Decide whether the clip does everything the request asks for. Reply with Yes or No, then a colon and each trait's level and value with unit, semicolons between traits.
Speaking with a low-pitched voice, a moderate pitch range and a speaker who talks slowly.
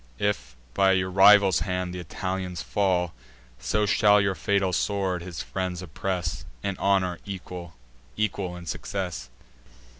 No: very low, 95 Hz; narrow, 1.9 semitones; slow, 130 wpm